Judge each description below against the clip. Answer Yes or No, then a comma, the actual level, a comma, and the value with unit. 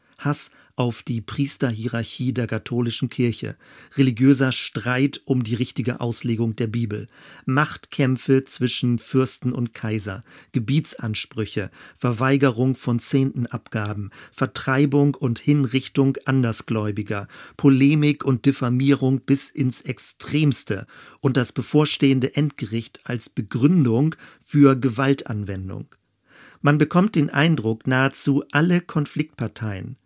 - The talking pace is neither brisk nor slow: No, slow, 100 wpm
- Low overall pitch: Yes, low, 130 Hz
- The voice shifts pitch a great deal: No, average, 3.0 semitones